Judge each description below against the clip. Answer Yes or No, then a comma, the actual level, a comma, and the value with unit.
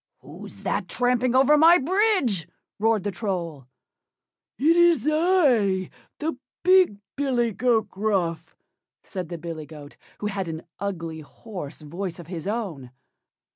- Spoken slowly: Yes, slow, 130 wpm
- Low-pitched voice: No, high, 205 Hz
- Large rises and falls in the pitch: Yes, wide, 8.1 semitones